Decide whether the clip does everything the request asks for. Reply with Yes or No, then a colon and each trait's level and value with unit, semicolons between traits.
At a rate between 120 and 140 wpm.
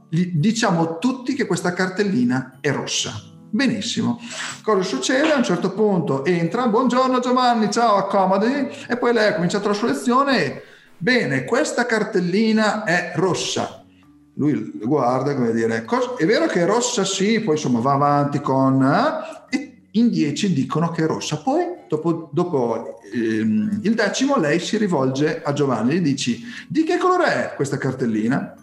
No: average, 155 wpm